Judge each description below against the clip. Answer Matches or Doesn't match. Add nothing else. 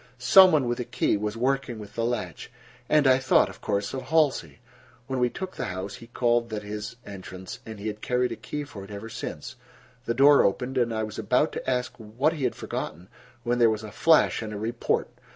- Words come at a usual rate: Doesn't match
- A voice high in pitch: Doesn't match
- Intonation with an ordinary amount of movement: Matches